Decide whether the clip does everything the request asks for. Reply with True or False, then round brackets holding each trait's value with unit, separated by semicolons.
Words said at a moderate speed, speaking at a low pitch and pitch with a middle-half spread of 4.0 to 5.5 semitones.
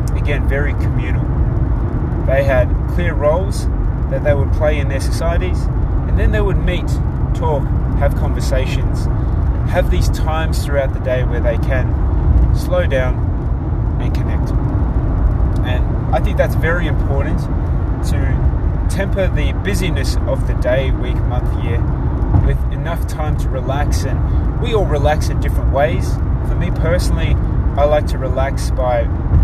True (145 wpm; 85 Hz; 5.0 semitones)